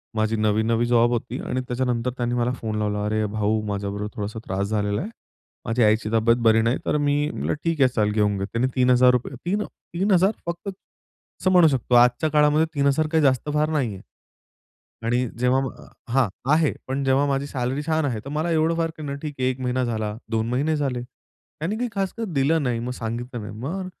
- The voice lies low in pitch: Yes, low, 125 Hz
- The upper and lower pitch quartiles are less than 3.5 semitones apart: No, average, 5.0 semitones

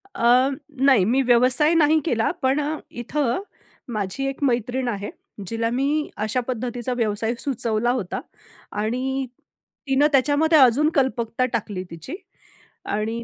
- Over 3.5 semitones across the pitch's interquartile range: No, average, 3.1 semitones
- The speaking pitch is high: Yes, very high, 250 Hz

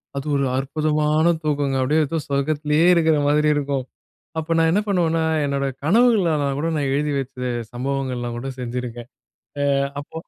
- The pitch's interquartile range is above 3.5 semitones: No, average, 2.8 semitones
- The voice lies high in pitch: No, medium, 145 Hz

